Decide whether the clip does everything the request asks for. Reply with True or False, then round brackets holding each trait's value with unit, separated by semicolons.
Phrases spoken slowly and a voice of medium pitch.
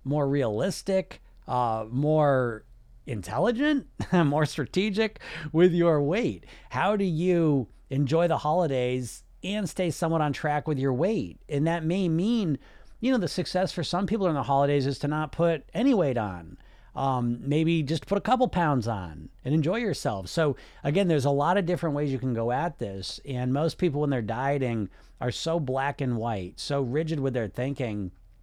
False (180 wpm; 150 Hz)